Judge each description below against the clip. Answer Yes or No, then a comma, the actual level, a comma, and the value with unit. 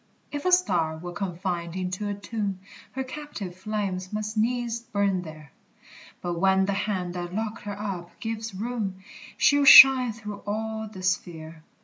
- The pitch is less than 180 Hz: No, high, 200 Hz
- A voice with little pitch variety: No, average, 3.4 semitones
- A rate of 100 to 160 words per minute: Yes, average, 155 wpm